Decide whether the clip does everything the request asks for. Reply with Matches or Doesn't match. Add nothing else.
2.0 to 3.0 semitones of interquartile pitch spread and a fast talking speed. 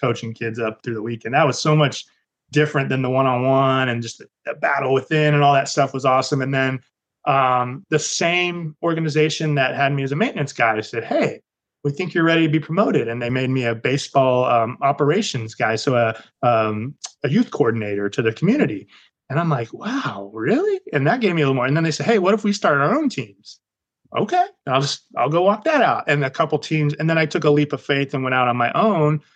Doesn't match